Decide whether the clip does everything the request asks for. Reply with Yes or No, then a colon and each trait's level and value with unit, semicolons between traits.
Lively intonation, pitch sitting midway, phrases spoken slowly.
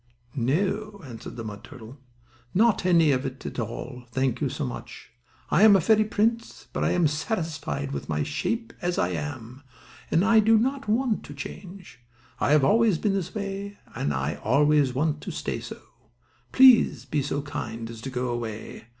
No: wide, 8.9 semitones; medium, 150 Hz; average, 175 wpm